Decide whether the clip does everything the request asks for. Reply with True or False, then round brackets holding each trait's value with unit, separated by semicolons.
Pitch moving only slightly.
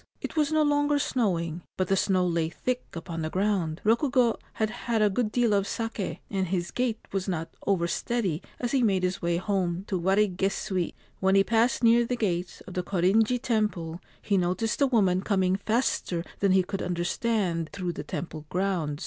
False (4.3 semitones)